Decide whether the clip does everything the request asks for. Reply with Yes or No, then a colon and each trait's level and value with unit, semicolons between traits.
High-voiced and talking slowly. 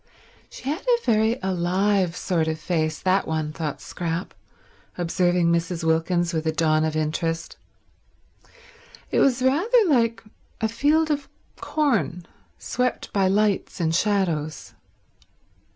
No: medium, 180 Hz; slow, 125 wpm